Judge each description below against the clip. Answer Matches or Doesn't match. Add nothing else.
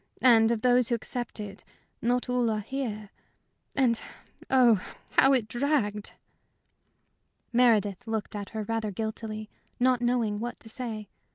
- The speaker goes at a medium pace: Doesn't match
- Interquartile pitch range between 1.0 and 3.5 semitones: Matches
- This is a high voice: Matches